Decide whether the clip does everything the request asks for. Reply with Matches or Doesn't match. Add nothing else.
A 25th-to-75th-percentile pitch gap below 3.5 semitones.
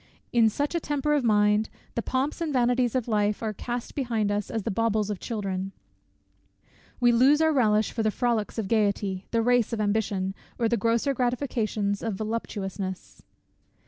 Matches